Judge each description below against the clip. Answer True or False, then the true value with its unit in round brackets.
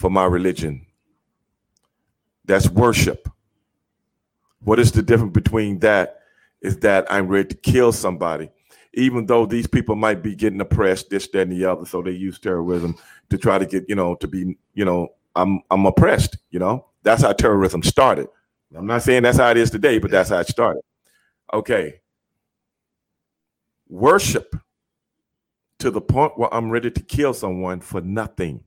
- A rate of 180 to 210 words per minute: False (165 wpm)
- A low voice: True (100 Hz)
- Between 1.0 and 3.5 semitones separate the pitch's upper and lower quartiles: False (3.9 semitones)